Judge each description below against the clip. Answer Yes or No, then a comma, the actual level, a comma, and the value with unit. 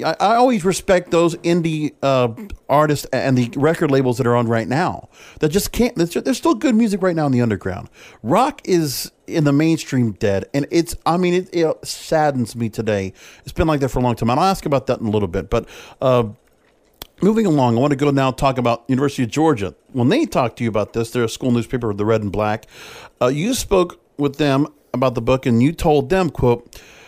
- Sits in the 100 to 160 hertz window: Yes, low, 135 Hz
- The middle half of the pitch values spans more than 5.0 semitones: Yes, wide, 5.4 semitones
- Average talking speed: No, fast, 225 wpm